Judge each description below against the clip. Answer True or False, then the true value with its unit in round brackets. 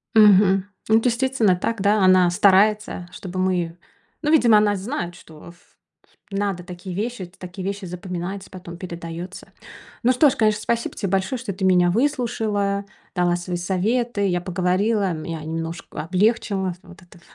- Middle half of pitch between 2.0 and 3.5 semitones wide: True (3.2 semitones)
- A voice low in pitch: False (190 Hz)